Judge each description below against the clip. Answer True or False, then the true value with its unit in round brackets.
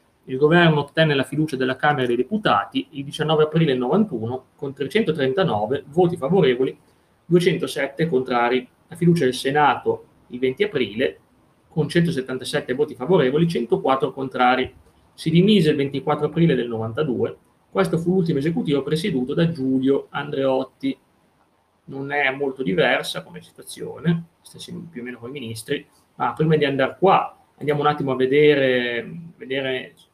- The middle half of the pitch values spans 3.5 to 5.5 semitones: True (4.6 semitones)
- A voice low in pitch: False (145 Hz)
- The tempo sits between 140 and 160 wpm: True (145 wpm)